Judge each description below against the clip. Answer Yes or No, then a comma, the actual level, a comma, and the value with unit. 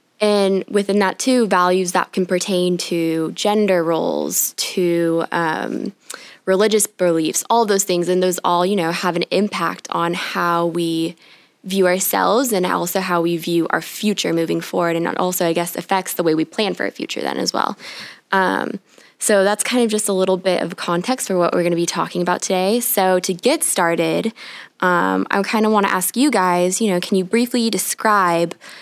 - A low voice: No, medium, 185 Hz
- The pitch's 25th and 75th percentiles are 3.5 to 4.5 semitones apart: No, average, 2.8 semitones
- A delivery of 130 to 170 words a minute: No, average, 200 wpm